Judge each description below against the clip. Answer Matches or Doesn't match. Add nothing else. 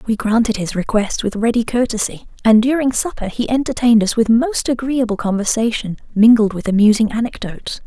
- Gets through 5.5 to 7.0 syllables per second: Matches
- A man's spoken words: Doesn't match